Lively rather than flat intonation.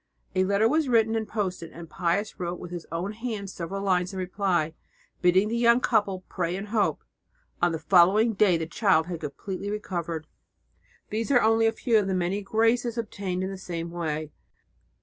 No: average, 3.9 semitones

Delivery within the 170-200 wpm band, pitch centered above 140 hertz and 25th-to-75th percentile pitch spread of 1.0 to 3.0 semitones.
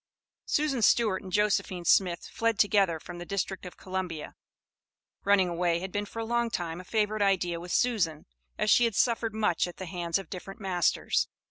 No: average, 190 wpm; high, 190 Hz; average, 3.4 semitones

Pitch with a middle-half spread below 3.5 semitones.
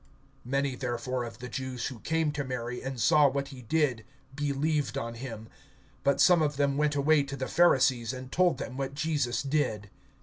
Yes: average, 2.8 semitones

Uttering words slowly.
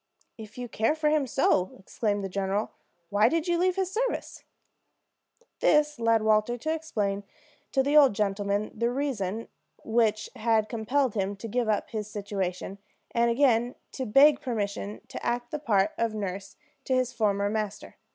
No: average, 165 wpm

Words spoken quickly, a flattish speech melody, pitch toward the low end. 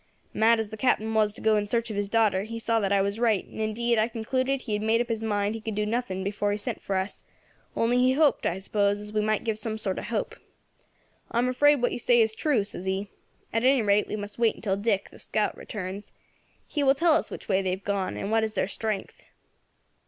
No: fast, 255 wpm; narrow, 2.3 semitones; high, 215 Hz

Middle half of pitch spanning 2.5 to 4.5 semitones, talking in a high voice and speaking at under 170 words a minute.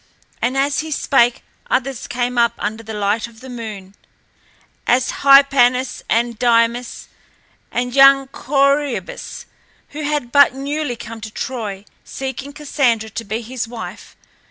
Yes: average, 3.1 semitones; high, 245 Hz; slow, 135 wpm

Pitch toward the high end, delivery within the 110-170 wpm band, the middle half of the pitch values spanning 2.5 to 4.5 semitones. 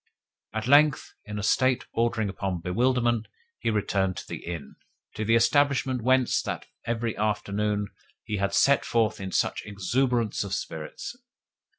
No: low, 110 Hz; average, 150 wpm; average, 3.6 semitones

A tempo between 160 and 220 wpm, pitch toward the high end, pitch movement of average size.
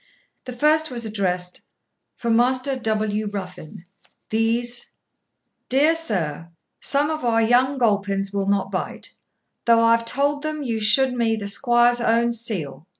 No: average, 140 wpm; high, 230 Hz; average, 3.6 semitones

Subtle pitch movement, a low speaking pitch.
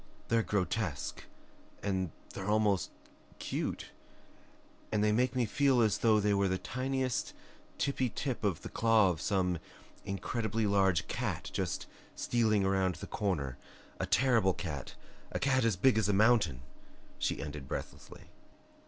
No: average, 3.6 semitones; low, 105 Hz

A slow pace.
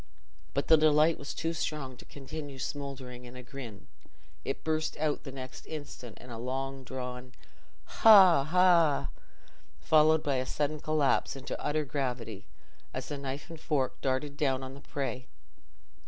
No: average, 155 wpm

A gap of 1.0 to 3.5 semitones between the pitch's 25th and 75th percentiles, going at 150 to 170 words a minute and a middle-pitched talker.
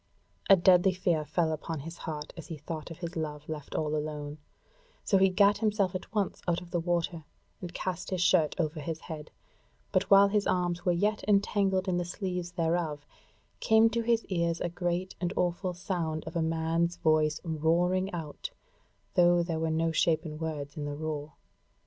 No: average, 2.7 semitones; average, 185 wpm; medium, 170 Hz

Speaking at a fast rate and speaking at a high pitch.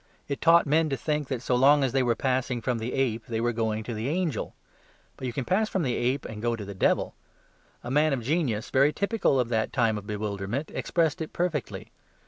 No: fast, 230 wpm; low, 130 Hz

